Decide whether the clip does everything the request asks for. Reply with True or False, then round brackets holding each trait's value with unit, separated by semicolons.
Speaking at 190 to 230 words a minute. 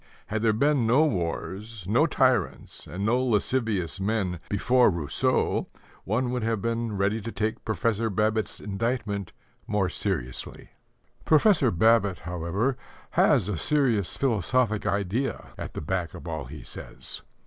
False (135 wpm)